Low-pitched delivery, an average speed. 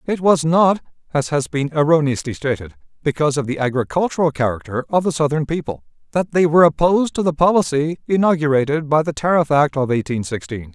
No: medium, 150 Hz; average, 180 wpm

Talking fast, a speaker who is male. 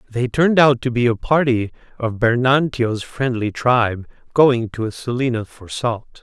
No: average, 165 wpm; male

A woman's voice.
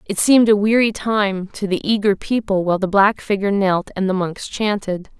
Yes: female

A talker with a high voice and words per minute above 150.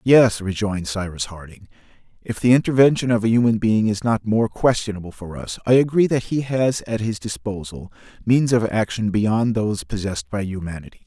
No: low, 110 Hz; average, 180 wpm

